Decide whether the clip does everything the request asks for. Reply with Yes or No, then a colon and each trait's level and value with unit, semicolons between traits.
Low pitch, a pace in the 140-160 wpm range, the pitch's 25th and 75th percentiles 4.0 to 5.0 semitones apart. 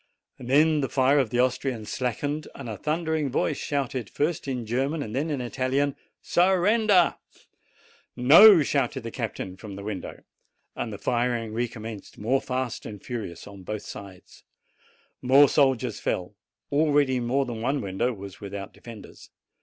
Yes: low, 125 Hz; average, 150 wpm; average, 4.4 semitones